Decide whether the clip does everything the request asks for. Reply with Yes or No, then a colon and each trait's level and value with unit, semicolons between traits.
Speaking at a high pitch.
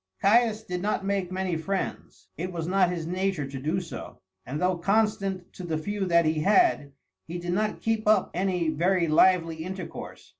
No: medium, 180 Hz